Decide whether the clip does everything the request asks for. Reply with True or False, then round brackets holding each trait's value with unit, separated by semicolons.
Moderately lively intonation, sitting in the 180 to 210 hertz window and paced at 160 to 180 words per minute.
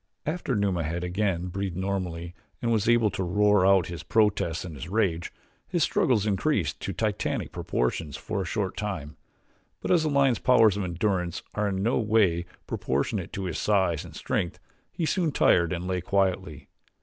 False (3.7 semitones; 95 Hz; 175 wpm)